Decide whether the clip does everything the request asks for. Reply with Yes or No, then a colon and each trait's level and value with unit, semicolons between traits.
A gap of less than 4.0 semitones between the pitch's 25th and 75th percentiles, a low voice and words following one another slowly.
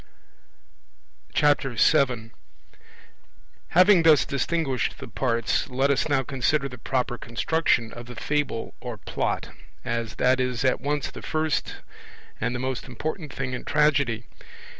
Yes: average, 3.5 semitones; low, 130 Hz; slow, 130 wpm